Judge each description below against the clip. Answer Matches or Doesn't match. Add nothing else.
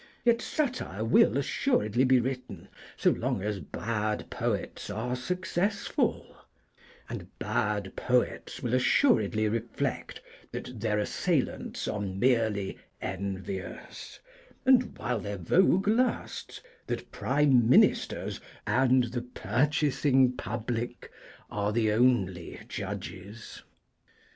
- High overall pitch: Doesn't match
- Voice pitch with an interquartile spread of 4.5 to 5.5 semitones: Doesn't match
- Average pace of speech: Doesn't match